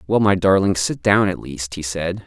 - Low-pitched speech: Yes, very low, 95 Hz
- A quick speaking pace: Yes, fast, 240 wpm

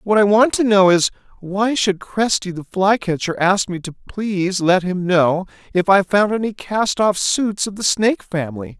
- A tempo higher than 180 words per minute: Yes, average, 200 wpm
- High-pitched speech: Yes, high, 195 Hz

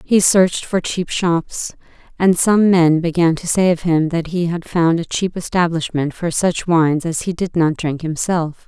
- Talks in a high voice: No, medium, 170 Hz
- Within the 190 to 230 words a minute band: Yes, average, 200 wpm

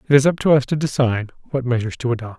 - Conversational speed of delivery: No, fast, 275 wpm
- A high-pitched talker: No, low, 130 Hz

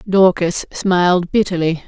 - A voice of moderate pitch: Yes, medium, 180 Hz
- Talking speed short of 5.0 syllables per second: Yes, 4.2 syllables/s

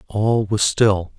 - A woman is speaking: No, male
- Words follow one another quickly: No, average, 150 wpm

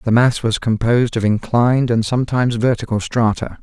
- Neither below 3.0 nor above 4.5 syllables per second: No, 5.7 syllables/s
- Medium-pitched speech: No, low, 115 Hz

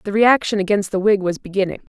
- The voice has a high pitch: Yes, high, 200 Hz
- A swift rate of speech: Yes, fast, 215 wpm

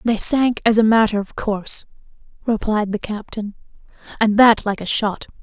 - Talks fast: No, average, 165 wpm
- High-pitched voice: Yes, high, 215 Hz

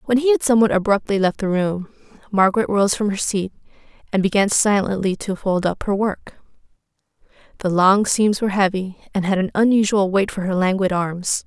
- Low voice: No, high, 200 Hz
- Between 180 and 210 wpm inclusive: Yes, average, 185 wpm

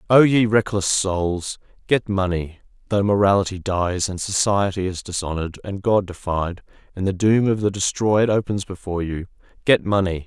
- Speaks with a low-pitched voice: Yes, very low, 95 Hz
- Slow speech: No, average, 145 wpm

